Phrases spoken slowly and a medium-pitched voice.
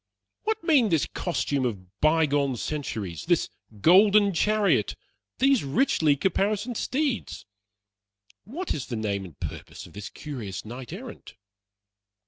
Yes: slow, 125 wpm; medium, 155 Hz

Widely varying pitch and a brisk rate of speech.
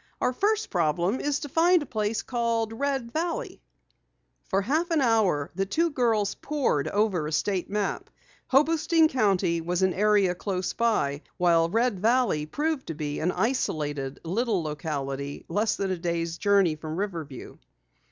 No: wide, 7.0 semitones; average, 155 wpm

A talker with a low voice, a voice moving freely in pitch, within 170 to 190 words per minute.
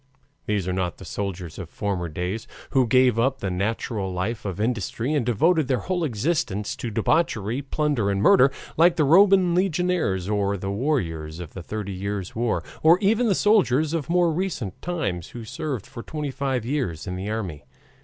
Yes: low, 115 Hz; wide, 7.9 semitones; average, 185 wpm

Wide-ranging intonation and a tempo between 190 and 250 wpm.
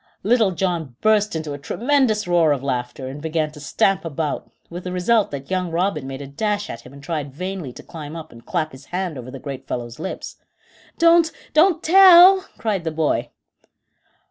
Yes: wide, 6.6 semitones; average, 195 wpm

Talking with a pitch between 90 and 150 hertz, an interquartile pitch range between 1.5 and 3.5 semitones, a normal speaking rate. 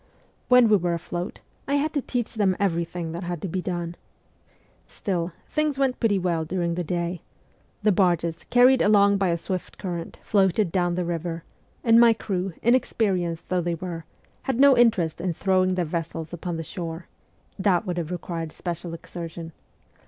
No: medium, 180 Hz; average, 3.2 semitones; average, 175 wpm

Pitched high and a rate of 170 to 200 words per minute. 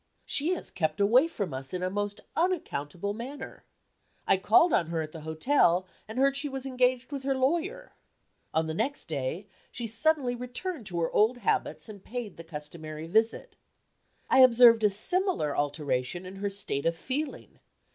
Yes: high, 215 Hz; average, 175 wpm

